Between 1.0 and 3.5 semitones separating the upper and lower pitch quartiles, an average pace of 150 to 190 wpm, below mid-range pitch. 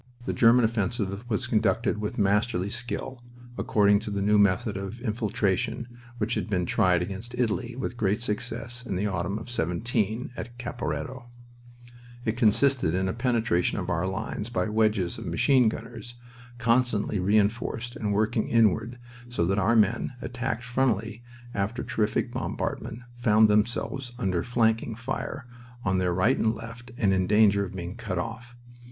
Yes: average, 3.2 semitones; average, 155 wpm; low, 110 Hz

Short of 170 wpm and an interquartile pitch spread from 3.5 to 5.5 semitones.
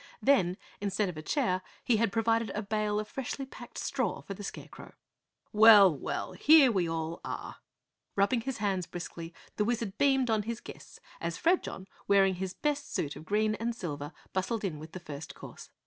No: average, 185 wpm; average, 4.2 semitones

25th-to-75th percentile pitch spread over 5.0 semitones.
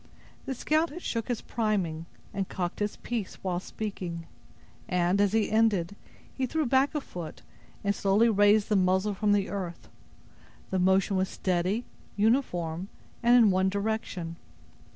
No: average, 3.3 semitones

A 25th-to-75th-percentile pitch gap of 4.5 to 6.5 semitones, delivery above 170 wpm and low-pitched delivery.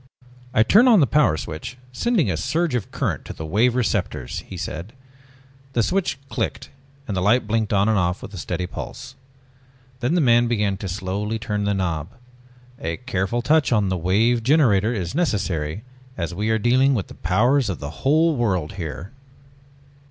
Yes: average, 5.3 semitones; average, 180 wpm; low, 105 Hz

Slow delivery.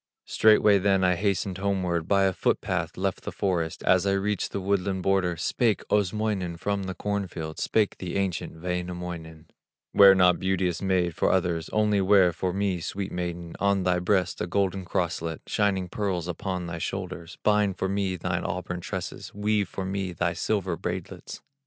No: average, 170 wpm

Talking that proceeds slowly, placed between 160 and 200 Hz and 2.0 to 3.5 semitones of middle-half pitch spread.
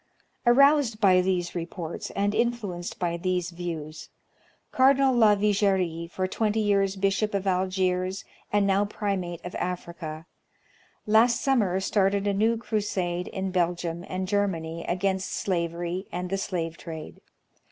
Yes: slow, 130 wpm; high, 190 Hz; average, 2.8 semitones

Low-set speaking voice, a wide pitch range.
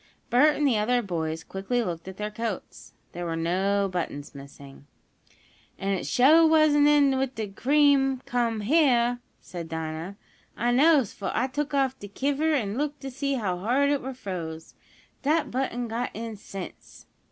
No: high, 235 Hz; wide, 6.4 semitones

